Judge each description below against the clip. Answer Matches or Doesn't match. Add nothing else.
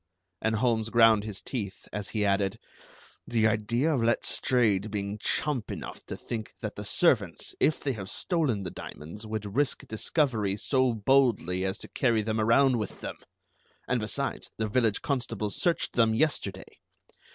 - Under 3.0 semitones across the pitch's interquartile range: Doesn't match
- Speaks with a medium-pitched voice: Doesn't match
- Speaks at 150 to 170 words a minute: Matches